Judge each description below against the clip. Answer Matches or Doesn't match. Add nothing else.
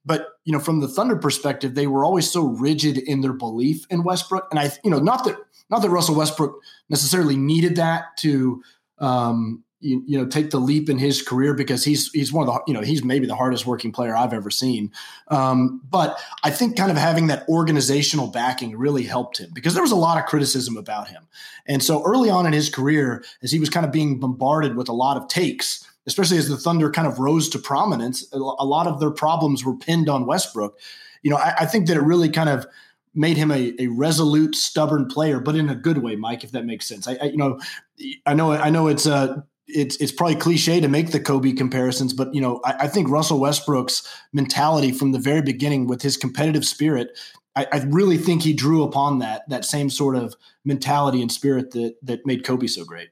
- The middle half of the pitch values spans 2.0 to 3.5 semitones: Matches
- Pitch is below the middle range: Doesn't match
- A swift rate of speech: Matches